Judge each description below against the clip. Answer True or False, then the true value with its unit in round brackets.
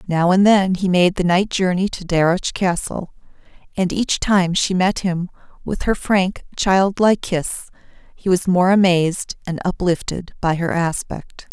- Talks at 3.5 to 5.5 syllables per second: True (4.4 syllables/s)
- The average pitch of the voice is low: False (185 Hz)